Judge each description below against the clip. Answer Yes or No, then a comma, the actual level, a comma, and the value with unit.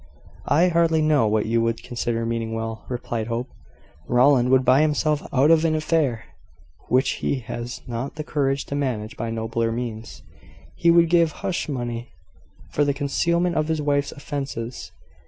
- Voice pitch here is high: No, low, 130 Hz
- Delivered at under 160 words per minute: No, average, 165 wpm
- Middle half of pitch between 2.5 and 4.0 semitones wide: No, average, 4.8 semitones